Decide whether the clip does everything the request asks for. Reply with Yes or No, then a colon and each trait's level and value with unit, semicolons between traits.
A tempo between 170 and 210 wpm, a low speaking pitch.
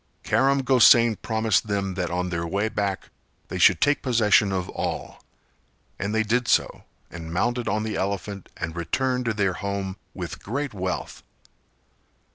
No: average, 155 wpm; low, 100 Hz